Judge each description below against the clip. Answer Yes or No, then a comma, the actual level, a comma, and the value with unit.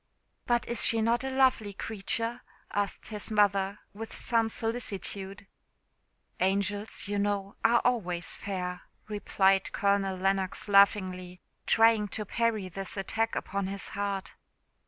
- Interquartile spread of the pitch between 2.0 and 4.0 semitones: Yes, narrow, 2.5 semitones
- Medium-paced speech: No, slow, 125 wpm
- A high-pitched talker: Yes, high, 200 Hz